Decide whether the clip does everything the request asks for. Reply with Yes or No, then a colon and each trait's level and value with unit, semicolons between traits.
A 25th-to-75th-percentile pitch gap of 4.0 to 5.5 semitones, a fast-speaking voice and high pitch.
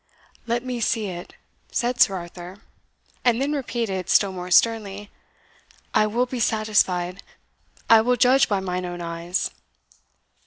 No: average, 4.7 semitones; average, 140 wpm; high, 210 Hz